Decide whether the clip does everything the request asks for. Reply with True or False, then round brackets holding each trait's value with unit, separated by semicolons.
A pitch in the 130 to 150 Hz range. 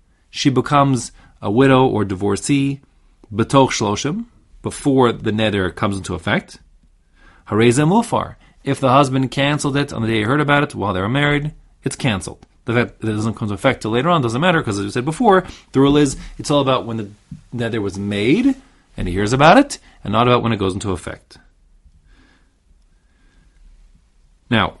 False (115 Hz)